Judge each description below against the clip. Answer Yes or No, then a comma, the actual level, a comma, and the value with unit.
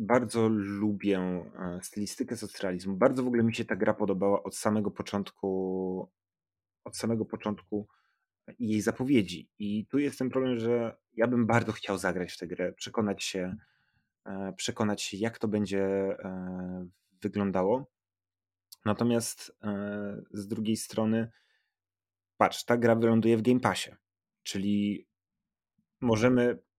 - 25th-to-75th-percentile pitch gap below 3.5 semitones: Yes, average, 3.0 semitones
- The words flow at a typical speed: Yes, average, 125 wpm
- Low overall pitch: Yes, low, 105 Hz